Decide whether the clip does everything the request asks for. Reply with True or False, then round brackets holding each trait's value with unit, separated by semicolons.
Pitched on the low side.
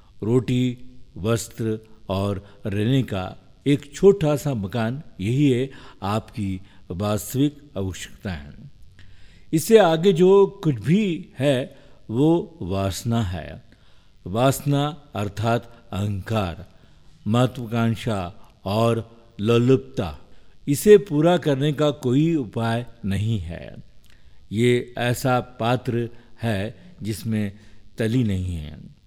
True (115 Hz)